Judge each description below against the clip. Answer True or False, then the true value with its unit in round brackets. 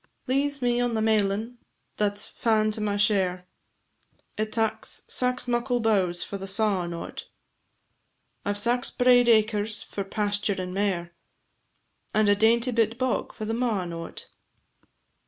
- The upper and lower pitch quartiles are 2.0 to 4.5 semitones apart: True (2.9 semitones)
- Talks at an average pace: True (150 wpm)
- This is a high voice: True (215 Hz)